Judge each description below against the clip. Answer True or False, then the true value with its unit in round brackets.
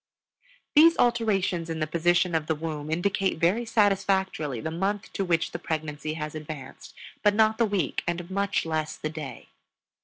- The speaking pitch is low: False (170 Hz)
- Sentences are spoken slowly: False (160 wpm)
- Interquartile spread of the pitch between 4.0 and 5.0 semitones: True (4.3 semitones)